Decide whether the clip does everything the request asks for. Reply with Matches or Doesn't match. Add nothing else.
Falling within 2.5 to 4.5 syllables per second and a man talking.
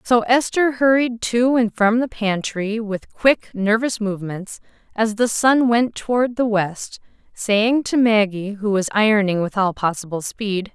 Doesn't match